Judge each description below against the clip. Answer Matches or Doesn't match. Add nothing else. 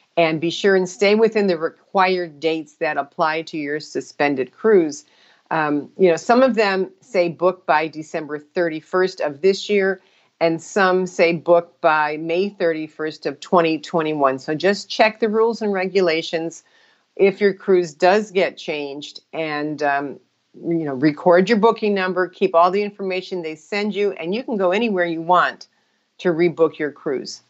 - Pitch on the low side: Doesn't match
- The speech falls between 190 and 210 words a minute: Doesn't match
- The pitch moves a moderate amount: Matches